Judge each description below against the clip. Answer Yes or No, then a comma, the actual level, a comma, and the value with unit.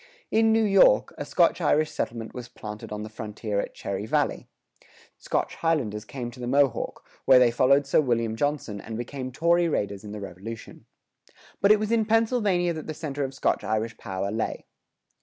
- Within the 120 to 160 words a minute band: No, average, 185 wpm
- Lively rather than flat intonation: Yes, wide, 6.6 semitones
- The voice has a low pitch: Yes, low, 125 Hz